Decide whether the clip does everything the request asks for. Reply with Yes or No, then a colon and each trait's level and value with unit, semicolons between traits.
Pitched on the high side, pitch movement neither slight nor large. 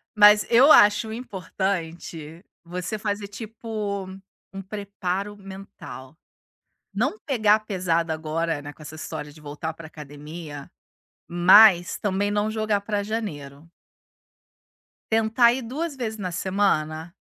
Yes: high, 195 Hz; average, 4.7 semitones